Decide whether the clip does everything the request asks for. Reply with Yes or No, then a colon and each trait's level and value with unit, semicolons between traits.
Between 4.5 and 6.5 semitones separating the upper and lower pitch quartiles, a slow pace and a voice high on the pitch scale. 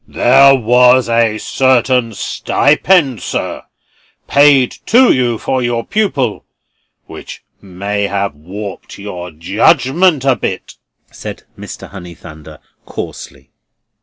No: average, 5.1 semitones; slow, 105 wpm; low, 120 Hz